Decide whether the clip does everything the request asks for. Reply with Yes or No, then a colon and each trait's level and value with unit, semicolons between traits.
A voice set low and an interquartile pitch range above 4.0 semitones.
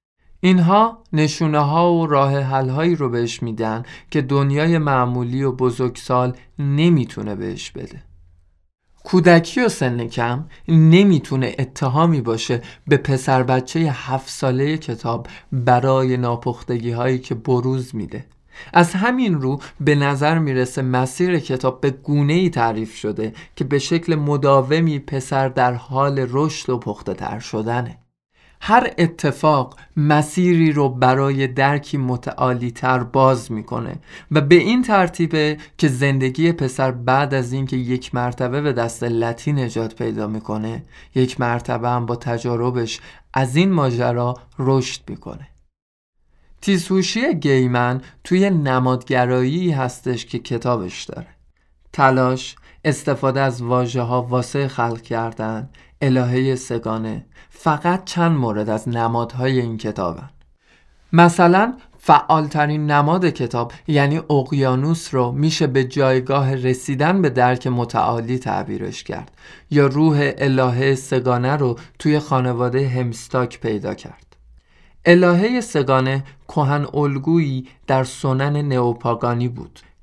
No: low, 130 Hz; average, 3.5 semitones